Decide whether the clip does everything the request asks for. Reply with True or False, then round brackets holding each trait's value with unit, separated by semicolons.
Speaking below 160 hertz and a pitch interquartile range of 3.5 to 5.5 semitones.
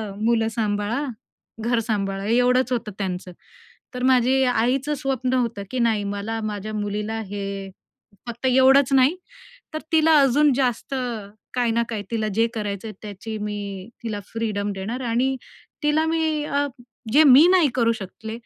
False (230 Hz; 4.0 semitones)